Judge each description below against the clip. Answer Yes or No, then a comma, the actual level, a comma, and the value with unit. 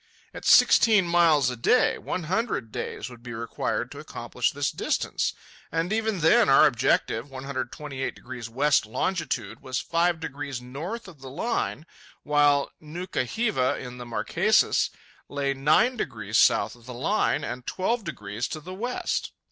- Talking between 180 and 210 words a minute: No, average, 150 wpm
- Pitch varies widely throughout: Yes, wide, 6.3 semitones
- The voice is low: No, medium, 145 Hz